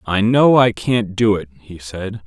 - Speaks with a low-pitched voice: Yes, low, 105 Hz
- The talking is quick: Yes, fast, 210 wpm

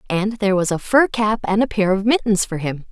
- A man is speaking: No, female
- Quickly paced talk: Yes, fast, 270 wpm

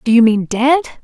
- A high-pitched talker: Yes, very high, 250 Hz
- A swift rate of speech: Yes, fast, 230 wpm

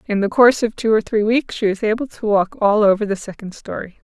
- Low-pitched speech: No, high, 215 Hz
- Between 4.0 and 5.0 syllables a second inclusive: No, 5.9 syllables/s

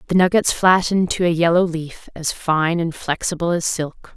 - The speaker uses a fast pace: No, average, 190 wpm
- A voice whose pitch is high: No, medium, 170 Hz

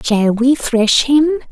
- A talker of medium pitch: No, very high, 260 Hz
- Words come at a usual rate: Yes, average, 160 wpm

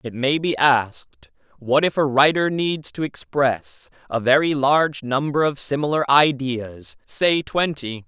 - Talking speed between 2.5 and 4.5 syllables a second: Yes, 4.1 syllables/s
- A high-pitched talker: No, low, 135 Hz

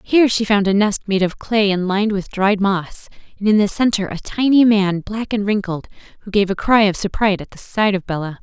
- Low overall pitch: No, high, 205 Hz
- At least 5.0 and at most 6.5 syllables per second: Yes, 5.6 syllables/s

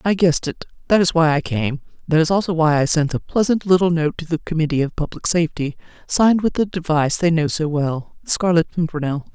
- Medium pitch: Yes, medium, 165 Hz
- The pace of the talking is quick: Yes, fast, 225 wpm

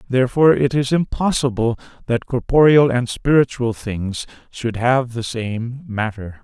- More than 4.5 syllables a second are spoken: No, 4.4 syllables/s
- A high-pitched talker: No, low, 125 Hz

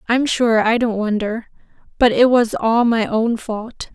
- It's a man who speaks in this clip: No, female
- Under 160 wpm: No, average, 180 wpm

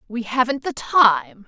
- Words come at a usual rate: Yes, average, 160 wpm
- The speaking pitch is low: No, high, 245 Hz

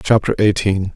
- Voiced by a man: Yes, male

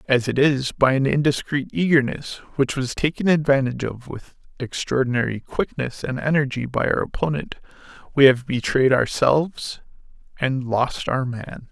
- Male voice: Yes, male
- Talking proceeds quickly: No, average, 145 wpm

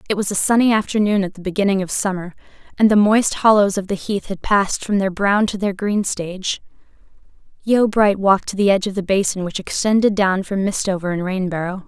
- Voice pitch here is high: Yes, high, 195 Hz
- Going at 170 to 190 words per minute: No, fast, 205 wpm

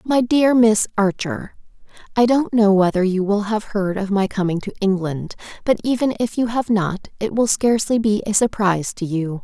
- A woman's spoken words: Yes, female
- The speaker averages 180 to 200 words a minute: Yes, average, 190 wpm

